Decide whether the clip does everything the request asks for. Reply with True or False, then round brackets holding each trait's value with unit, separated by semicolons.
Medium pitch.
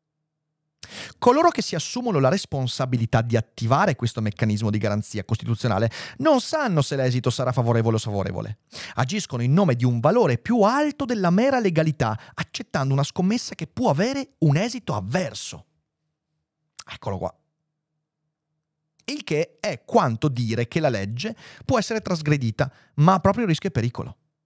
True (155 Hz)